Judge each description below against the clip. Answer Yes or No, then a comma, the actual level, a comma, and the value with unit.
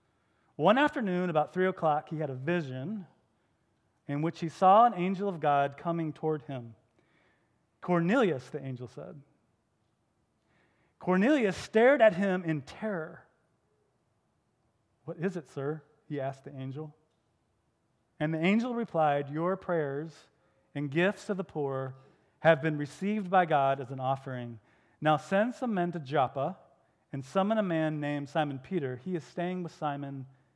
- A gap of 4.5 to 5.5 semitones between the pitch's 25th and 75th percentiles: Yes, average, 4.9 semitones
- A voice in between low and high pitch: Yes, medium, 155 Hz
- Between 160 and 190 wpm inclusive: No, average, 145 wpm